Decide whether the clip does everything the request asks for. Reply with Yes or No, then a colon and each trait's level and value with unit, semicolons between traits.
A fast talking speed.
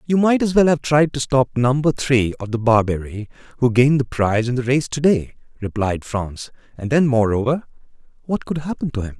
Yes: fast, 210 wpm